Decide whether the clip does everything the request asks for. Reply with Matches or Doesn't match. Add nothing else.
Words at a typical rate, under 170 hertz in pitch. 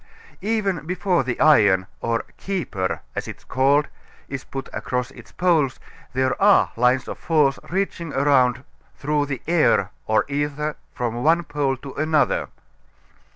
Matches